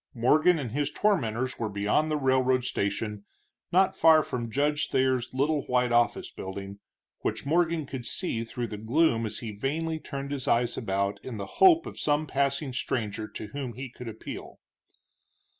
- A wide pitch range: No, average, 4.6 semitones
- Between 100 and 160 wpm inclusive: No, average, 170 wpm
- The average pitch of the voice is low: Yes, low, 130 Hz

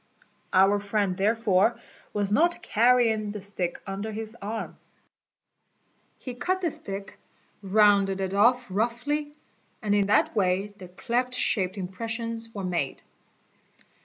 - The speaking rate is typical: No, slow, 125 wpm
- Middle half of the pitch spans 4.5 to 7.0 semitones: No, average, 3.0 semitones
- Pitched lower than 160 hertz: No, high, 210 Hz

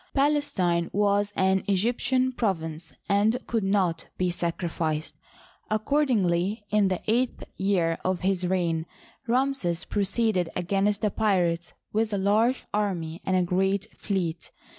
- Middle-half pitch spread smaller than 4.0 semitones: Yes, average, 3.6 semitones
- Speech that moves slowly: Yes, slow, 125 wpm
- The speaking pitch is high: Yes, high, 195 Hz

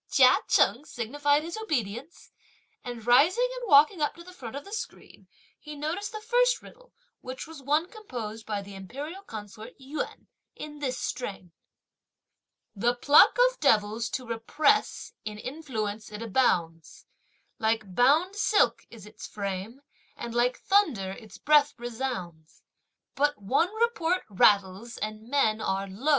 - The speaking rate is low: No, average, 145 wpm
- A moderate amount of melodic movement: No, wide, 6.4 semitones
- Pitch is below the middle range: No, very high, 250 Hz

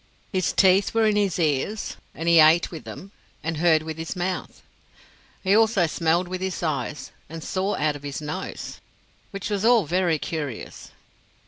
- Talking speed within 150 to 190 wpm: Yes, average, 175 wpm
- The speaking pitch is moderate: Yes, medium, 175 Hz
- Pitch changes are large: No, average, 3.5 semitones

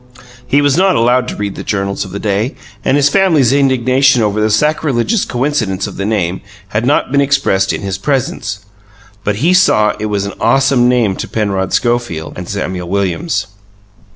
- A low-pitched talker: Yes, low, 115 Hz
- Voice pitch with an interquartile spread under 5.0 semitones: No, wide, 5.5 semitones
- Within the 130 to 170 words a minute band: No, average, 185 wpm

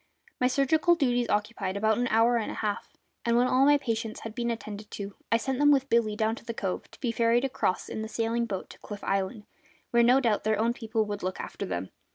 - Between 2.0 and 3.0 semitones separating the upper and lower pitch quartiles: Yes, narrow, 2.6 semitones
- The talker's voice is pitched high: Yes, high, 230 Hz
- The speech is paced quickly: Yes, fast, 240 wpm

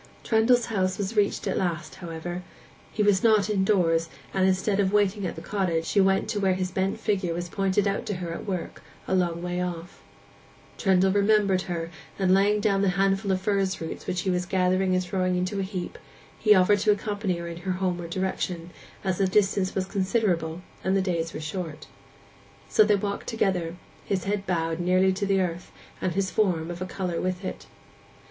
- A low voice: No, high, 190 Hz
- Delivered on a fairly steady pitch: Yes, narrow, 2.1 semitones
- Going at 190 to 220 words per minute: Yes, average, 200 wpm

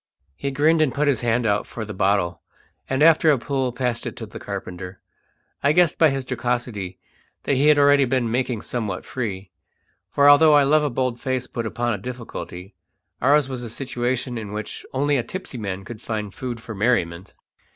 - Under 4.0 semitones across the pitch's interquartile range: No, average, 4.4 semitones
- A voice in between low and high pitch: No, low, 125 Hz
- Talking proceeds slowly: No, average, 195 wpm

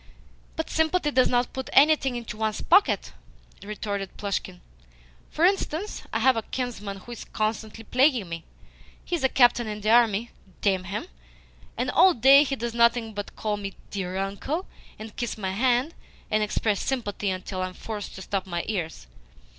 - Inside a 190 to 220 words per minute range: No, average, 175 wpm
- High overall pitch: Yes, high, 220 Hz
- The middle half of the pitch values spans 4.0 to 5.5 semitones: Yes, average, 4.4 semitones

